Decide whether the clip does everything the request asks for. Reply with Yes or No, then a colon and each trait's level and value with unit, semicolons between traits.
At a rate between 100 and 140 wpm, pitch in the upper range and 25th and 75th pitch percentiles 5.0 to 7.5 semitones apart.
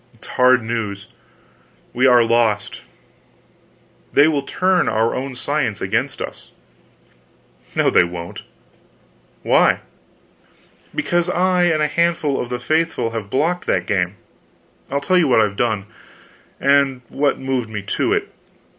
No: slow, 135 wpm; low, 130 Hz; wide, 5.5 semitones